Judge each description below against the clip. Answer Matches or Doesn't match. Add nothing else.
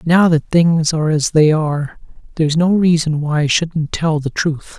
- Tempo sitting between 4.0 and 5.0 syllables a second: Matches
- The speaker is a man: Matches